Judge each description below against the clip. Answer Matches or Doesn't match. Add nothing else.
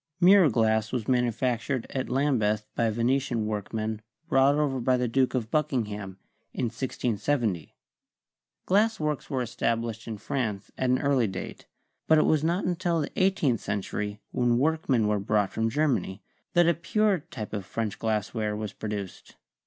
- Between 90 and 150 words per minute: Doesn't match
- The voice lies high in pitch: Doesn't match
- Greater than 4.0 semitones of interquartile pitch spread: Matches